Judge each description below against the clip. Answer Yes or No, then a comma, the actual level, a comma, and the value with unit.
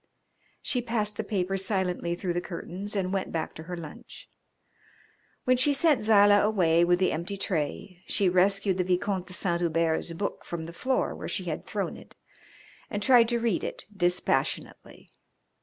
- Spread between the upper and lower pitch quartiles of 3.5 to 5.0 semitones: No, average, 3.1 semitones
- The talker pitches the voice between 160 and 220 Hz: Yes, high, 190 Hz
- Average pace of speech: Yes, average, 175 wpm